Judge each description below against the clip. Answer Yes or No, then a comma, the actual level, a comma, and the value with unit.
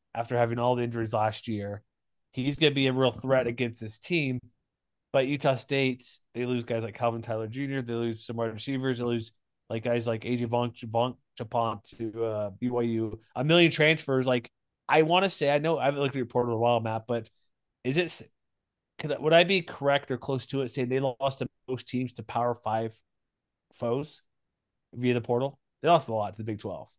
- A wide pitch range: No, average, 2.9 semitones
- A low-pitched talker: Yes, low, 125 Hz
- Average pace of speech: No, fast, 210 wpm